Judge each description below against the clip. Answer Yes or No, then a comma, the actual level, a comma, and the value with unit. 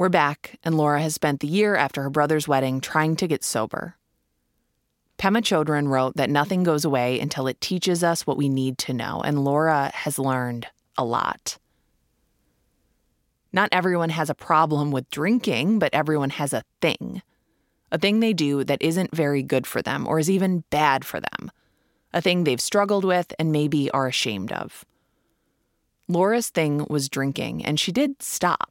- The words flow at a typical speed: Yes, average, 175 wpm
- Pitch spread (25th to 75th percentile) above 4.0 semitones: Yes, average, 4.7 semitones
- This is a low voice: No, medium, 150 Hz